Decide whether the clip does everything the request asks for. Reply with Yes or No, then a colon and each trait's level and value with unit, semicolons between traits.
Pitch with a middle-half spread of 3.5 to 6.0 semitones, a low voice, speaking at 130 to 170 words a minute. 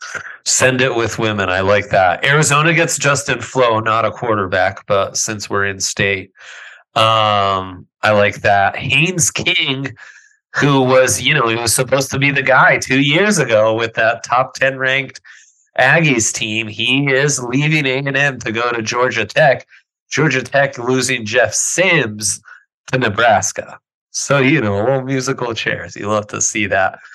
Yes: average, 4.3 semitones; low, 130 Hz; average, 165 wpm